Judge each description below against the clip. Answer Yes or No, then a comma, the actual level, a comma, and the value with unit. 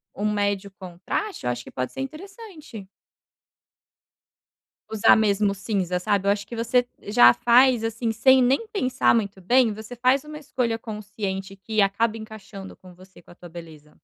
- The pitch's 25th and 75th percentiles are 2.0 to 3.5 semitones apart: No, average, 4.2 semitones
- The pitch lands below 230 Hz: Yes, high, 215 Hz